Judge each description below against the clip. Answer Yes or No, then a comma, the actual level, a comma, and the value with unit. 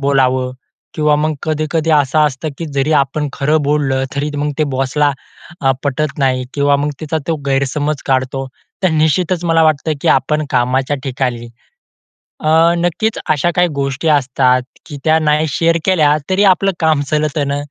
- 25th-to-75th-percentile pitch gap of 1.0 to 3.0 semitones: Yes, narrow, 2.6 semitones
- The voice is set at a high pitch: No, medium, 150 Hz